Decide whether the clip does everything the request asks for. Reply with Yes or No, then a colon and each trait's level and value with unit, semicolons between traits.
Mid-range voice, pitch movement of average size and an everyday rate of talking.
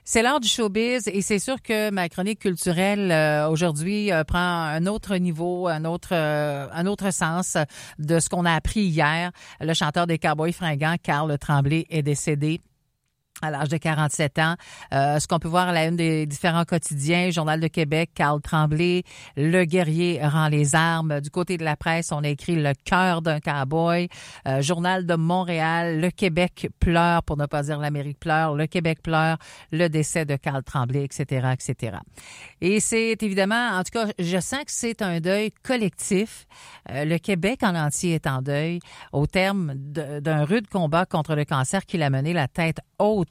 Yes: medium, 165 Hz; average, 3.3 semitones; average, 185 wpm